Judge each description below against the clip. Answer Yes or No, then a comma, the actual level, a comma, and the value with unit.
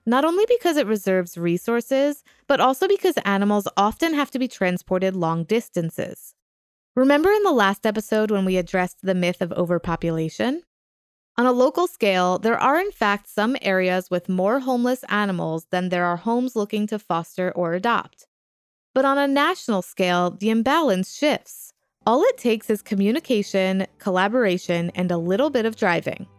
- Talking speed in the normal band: Yes, average, 165 wpm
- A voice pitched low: No, high, 205 Hz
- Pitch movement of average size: No, wide, 6.1 semitones